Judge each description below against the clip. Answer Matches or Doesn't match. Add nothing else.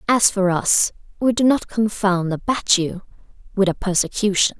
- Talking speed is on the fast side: Doesn't match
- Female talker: Matches